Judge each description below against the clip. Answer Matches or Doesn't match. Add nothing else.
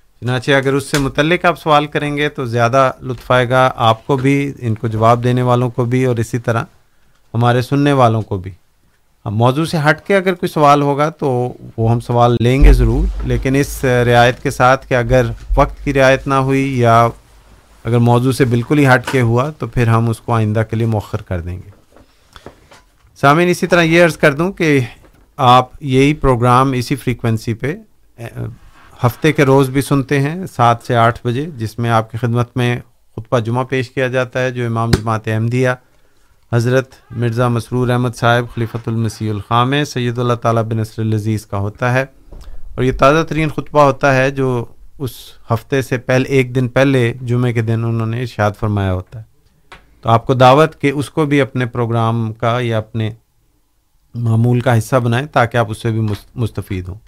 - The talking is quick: Matches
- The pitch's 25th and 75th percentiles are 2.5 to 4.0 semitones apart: Matches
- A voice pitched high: Doesn't match